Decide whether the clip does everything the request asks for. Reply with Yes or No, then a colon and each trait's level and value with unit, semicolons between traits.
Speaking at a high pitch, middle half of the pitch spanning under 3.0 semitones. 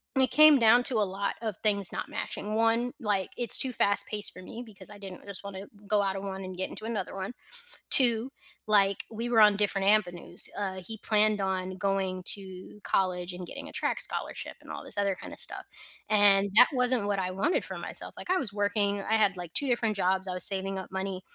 Yes: high, 200 Hz; narrow, 2.5 semitones